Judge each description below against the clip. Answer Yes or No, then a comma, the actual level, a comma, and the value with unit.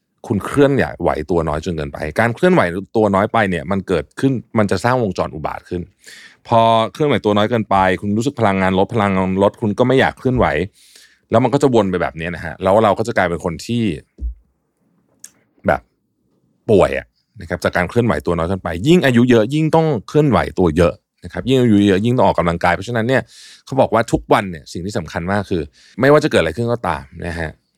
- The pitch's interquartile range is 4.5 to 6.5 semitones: Yes, average, 5.1 semitones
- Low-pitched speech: Yes, low, 100 Hz